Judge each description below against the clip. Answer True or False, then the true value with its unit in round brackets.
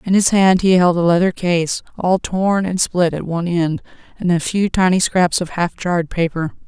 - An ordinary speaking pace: False (215 wpm)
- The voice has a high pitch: False (175 Hz)